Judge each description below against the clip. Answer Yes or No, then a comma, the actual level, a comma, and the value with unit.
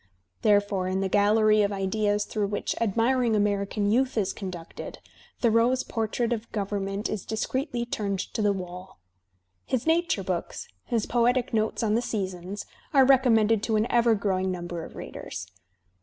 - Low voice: No, high, 215 Hz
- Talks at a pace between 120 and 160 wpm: Yes, average, 155 wpm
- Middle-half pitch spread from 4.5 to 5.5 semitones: No, average, 2.9 semitones